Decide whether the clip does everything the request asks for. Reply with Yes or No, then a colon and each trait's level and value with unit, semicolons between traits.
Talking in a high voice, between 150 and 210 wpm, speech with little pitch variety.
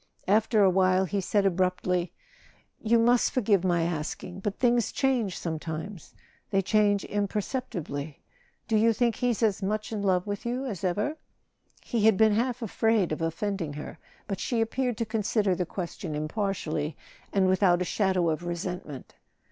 No: high, 195 Hz; average, 165 wpm; average, 3.9 semitones